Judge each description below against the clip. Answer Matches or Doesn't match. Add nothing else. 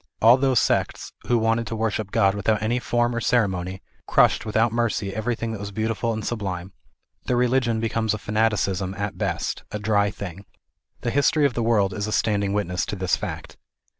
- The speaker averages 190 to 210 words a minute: Matches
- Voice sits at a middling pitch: Doesn't match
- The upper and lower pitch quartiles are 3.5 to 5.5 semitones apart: Doesn't match